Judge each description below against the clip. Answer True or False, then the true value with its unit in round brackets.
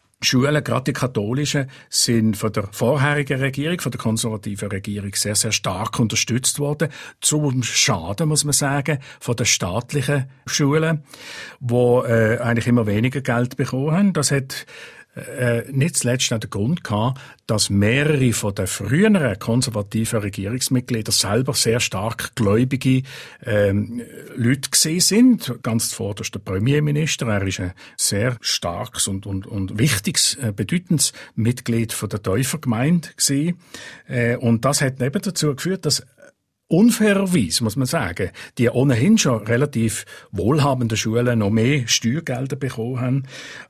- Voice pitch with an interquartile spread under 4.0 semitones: False (4.4 semitones)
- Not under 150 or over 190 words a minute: False (135 wpm)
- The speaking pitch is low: True (125 Hz)